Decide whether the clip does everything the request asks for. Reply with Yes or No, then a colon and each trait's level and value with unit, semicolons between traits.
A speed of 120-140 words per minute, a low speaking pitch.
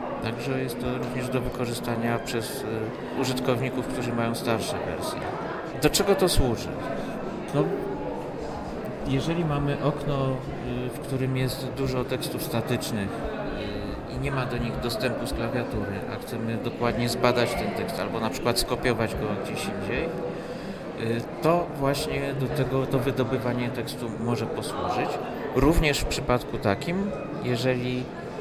Yes: average, 130 wpm; low, 130 Hz